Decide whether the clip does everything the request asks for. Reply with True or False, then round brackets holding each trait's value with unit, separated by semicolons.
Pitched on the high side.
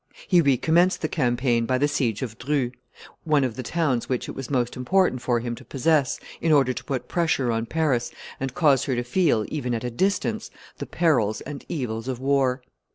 False (130 Hz)